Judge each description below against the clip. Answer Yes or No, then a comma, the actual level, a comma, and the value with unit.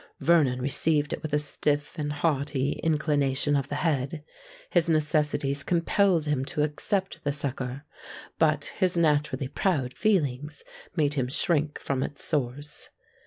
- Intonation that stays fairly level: Yes, narrow, 2.2 semitones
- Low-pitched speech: No, medium, 150 Hz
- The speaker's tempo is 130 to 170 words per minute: Yes, slow, 135 wpm